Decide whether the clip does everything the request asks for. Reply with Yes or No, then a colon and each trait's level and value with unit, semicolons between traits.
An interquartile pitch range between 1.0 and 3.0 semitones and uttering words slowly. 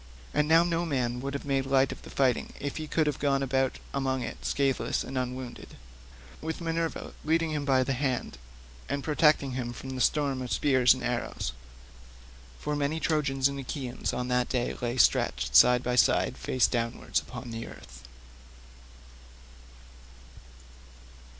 No: average, 2.7 semitones; average, 160 wpm